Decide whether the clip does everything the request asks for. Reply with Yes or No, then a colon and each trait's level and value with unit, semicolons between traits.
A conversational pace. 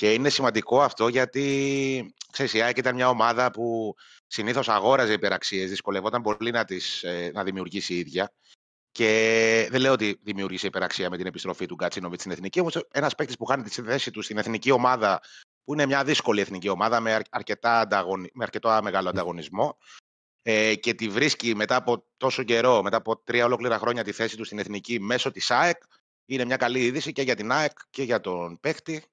No: fast, 185 wpm